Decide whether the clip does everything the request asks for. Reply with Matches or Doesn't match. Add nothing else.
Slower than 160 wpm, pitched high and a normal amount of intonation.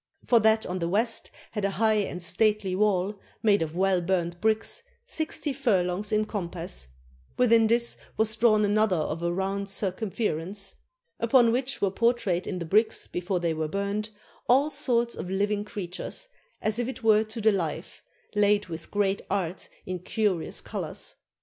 Doesn't match